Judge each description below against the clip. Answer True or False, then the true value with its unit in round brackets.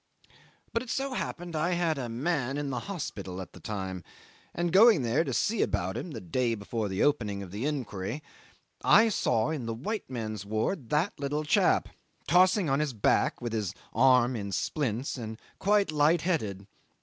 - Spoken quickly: False (185 wpm)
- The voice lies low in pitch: True (130 Hz)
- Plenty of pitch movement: True (7.4 semitones)